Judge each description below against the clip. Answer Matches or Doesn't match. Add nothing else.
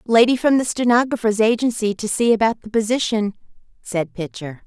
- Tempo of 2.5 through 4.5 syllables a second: Doesn't match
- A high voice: Matches